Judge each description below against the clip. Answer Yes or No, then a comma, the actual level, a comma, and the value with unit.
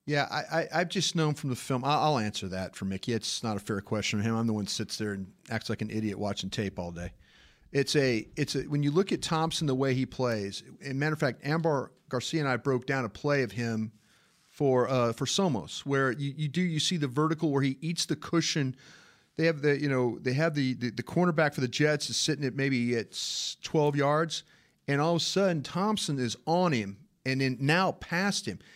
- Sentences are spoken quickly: Yes, fast, 240 wpm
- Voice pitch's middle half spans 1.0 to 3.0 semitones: No, average, 5.2 semitones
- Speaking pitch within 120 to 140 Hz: Yes, low, 135 Hz